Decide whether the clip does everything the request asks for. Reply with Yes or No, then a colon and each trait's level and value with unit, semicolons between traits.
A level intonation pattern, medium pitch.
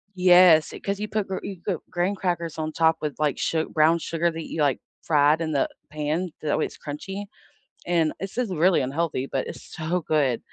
No: average, 3.0 semitones; medium, 165 Hz